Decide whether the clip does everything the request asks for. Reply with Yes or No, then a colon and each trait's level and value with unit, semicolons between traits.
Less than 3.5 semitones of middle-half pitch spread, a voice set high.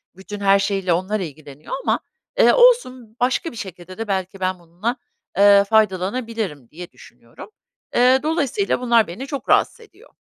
No: average, 5.1 semitones; high, 205 Hz